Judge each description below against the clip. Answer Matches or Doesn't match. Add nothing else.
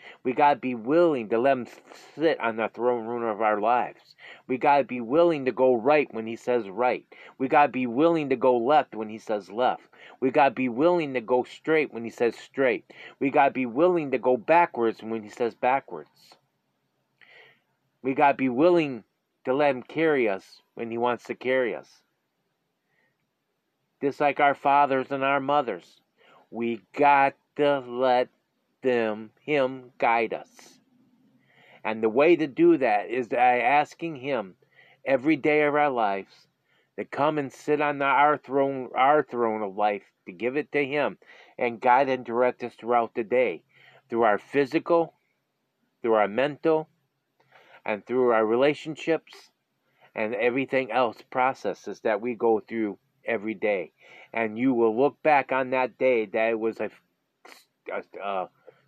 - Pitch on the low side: Matches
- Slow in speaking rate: Doesn't match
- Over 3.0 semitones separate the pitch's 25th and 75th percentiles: Matches